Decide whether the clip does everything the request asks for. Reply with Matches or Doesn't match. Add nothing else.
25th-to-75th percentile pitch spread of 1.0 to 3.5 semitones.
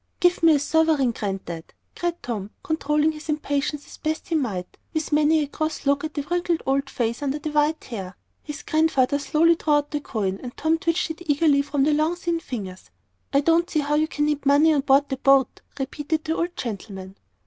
Matches